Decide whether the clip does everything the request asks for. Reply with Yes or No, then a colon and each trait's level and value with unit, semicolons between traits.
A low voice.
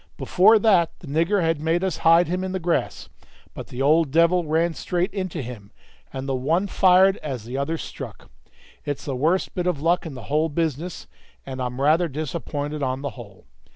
No: medium, 160 Hz